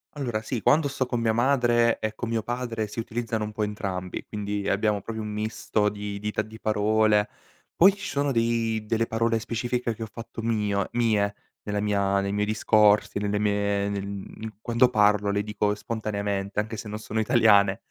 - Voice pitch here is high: No, low, 110 Hz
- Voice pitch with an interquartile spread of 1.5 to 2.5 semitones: Yes, narrow, 2.0 semitones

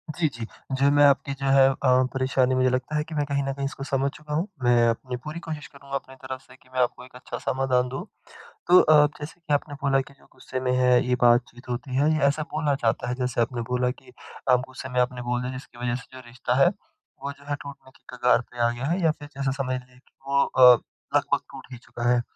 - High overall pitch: No, low, 130 Hz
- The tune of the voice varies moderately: No, narrow, 2.1 semitones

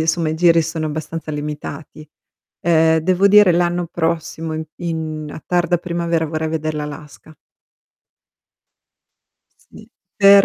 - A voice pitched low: No, medium, 160 Hz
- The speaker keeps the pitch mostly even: Yes, narrow, 1.7 semitones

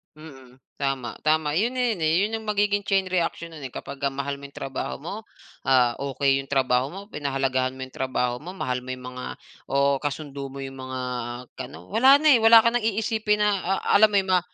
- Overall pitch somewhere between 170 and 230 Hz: No, medium, 145 Hz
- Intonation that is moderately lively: No, wide, 7.3 semitones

